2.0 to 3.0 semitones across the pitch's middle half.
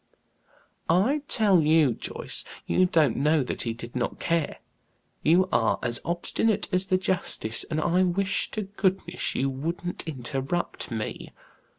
No: wide, 5.6 semitones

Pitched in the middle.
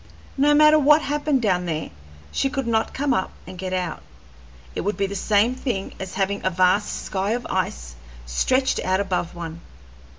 No: high, 200 Hz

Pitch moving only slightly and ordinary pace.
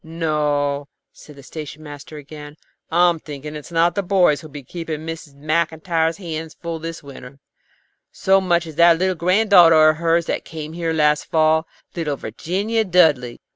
Yes: narrow, 2.2 semitones; average, 170 wpm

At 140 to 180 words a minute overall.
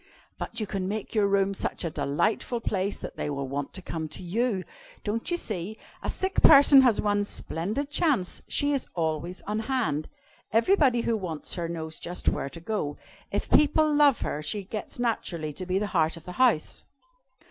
No: average, 190 wpm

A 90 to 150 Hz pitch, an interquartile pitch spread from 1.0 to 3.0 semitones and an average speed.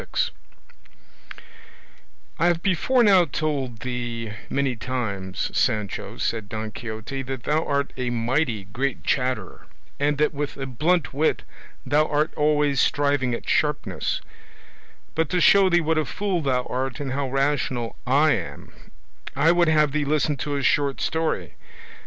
No: medium, 140 Hz; average, 3.7 semitones; average, 145 wpm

